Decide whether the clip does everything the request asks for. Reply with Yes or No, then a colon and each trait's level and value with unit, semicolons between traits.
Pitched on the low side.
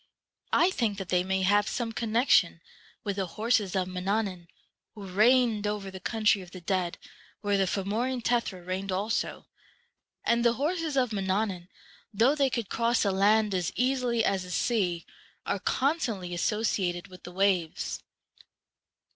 No: high, 205 Hz